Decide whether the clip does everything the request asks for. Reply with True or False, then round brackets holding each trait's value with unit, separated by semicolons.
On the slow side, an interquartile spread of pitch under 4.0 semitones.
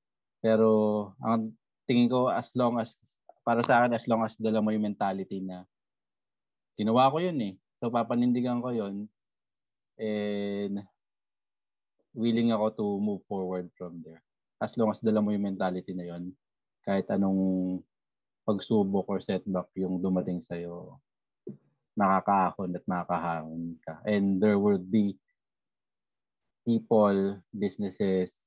True (130 wpm; 3.2 semitones)